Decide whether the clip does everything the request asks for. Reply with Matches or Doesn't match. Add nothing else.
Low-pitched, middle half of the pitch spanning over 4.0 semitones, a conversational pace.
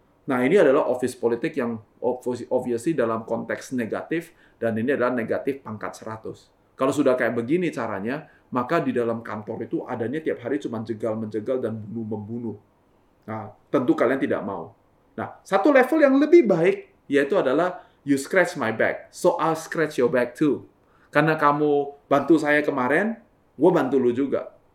Doesn't match